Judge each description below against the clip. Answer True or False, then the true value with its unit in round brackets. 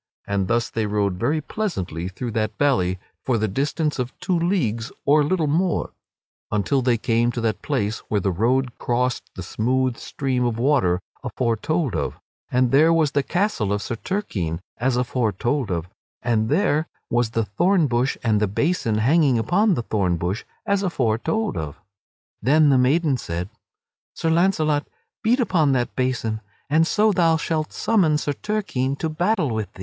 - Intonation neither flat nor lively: False (6.4 semitones)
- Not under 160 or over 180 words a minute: True (175 wpm)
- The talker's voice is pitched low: True (130 Hz)